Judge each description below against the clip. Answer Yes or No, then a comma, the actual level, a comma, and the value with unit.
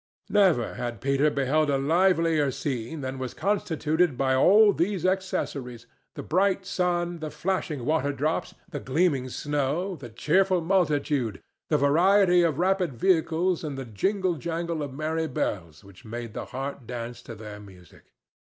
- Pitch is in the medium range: Yes, medium, 150 Hz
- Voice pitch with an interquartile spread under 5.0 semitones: No, average, 5.3 semitones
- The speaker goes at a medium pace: Yes, average, 150 wpm